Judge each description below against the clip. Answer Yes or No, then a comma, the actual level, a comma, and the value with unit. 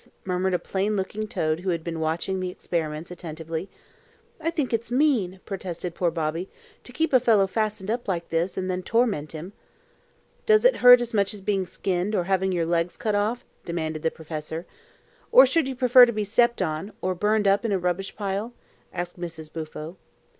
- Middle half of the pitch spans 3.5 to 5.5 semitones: Yes, average, 4.3 semitones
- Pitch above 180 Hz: Yes, high, 190 Hz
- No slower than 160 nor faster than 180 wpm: No, average, 195 wpm